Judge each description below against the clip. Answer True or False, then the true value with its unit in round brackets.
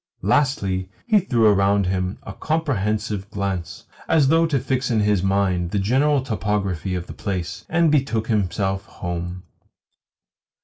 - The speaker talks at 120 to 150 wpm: True (140 wpm)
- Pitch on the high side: False (105 Hz)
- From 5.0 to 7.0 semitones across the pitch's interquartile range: True (5.6 semitones)